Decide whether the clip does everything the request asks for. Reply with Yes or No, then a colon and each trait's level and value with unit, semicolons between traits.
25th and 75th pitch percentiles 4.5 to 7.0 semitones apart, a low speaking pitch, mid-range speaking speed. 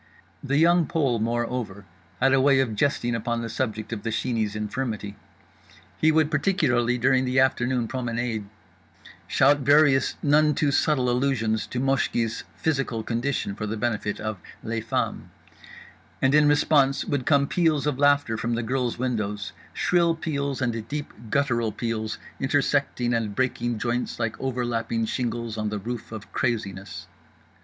No: average, 3.6 semitones; low, 125 Hz; average, 150 wpm